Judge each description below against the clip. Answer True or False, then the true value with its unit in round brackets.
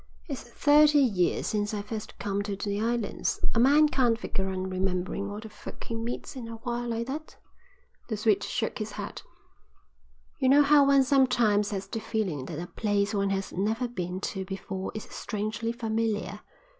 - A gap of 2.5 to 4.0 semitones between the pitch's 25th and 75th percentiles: True (3.2 semitones)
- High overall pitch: True (220 Hz)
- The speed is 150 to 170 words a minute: False (180 wpm)